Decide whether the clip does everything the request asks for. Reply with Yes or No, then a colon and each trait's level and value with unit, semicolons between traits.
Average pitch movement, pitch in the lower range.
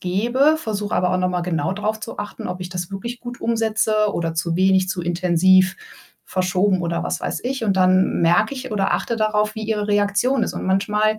No: average, 3.0 semitones; high, 200 Hz